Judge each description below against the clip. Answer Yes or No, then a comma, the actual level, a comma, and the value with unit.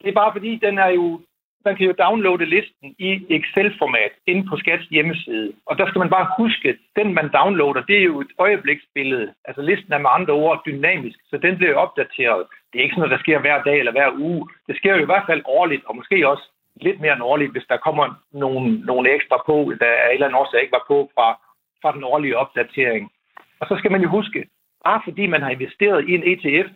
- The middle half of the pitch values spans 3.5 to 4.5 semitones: No, average, 5.1 semitones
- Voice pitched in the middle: Yes, medium, 180 Hz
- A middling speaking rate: No, fast, 235 wpm